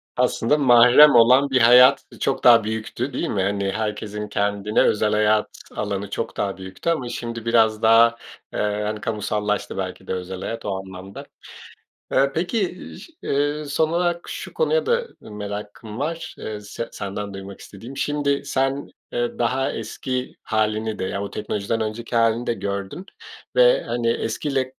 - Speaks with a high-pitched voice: No, low, 115 Hz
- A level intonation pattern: No, average, 4.3 semitones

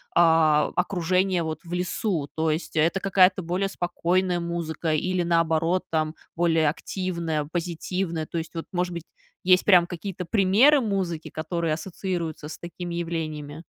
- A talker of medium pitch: Yes, medium, 170 Hz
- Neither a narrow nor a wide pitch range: No, narrow, 2.2 semitones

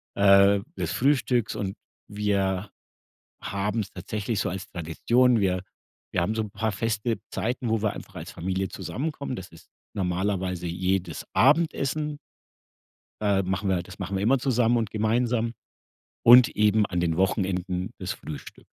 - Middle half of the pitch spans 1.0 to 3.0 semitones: No, average, 3.7 semitones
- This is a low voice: Yes, low, 100 Hz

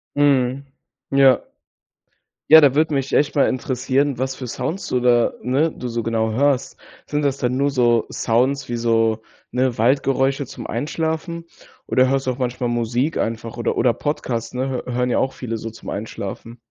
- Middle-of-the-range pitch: No, low, 130 Hz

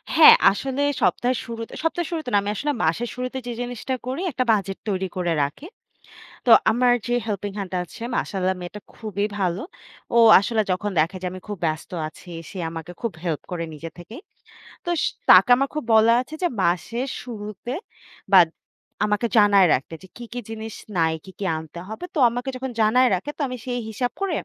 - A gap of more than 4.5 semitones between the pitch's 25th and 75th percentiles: Yes, average, 5.0 semitones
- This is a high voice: Yes, high, 215 Hz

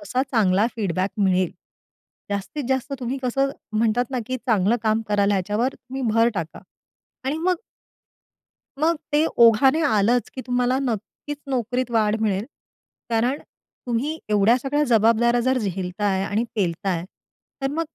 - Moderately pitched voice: No, high, 230 Hz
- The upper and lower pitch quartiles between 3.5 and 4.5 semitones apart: Yes, average, 4.2 semitones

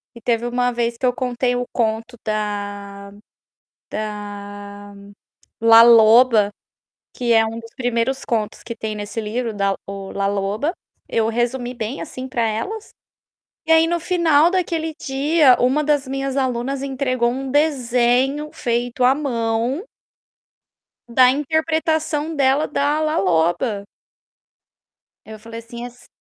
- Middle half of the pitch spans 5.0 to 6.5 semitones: No, average, 3.8 semitones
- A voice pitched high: Yes, high, 245 Hz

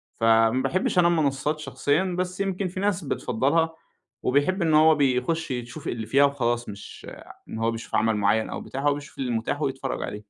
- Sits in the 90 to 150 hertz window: Yes, medium, 140 Hz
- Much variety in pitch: Yes, wide, 5.7 semitones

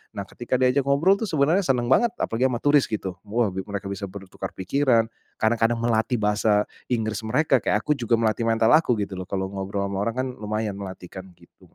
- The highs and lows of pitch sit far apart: No, average, 4.4 semitones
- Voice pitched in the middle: No, low, 115 Hz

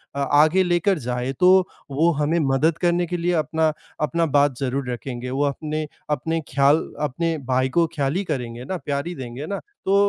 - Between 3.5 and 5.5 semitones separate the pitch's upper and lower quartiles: Yes, average, 4.0 semitones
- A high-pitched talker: No, medium, 150 Hz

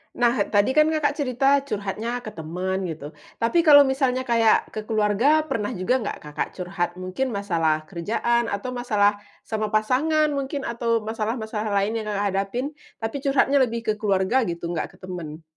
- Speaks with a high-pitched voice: Yes, high, 220 Hz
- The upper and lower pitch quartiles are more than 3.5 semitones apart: Yes, average, 4.8 semitones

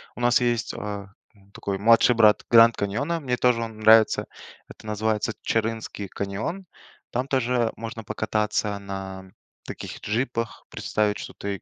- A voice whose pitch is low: Yes, low, 110 Hz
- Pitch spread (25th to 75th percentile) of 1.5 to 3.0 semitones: Yes, narrow, 2.4 semitones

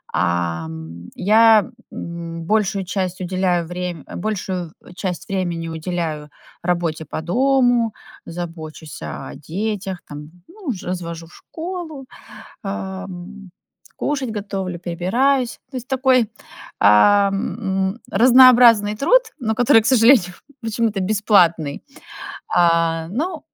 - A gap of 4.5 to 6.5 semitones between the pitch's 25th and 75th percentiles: Yes, average, 5.3 semitones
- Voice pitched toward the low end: No, high, 190 Hz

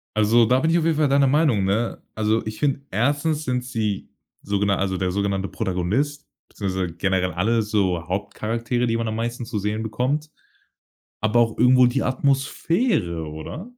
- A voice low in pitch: Yes, low, 115 Hz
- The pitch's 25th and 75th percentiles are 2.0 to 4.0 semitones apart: No, average, 5.2 semitones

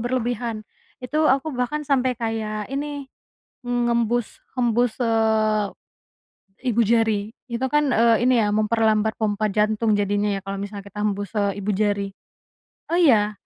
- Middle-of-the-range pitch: No, high, 220 Hz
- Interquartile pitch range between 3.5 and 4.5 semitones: No, average, 2.8 semitones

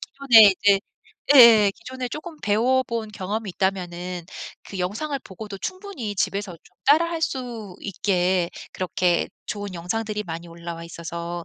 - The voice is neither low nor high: No, high, 205 Hz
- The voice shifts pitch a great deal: No, average, 4.7 semitones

